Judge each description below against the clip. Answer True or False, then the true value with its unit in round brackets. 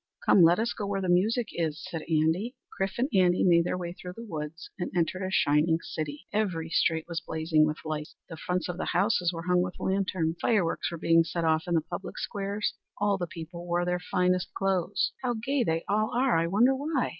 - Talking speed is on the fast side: True (220 wpm)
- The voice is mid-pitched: True (180 Hz)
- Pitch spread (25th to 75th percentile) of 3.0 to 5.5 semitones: True (3.3 semitones)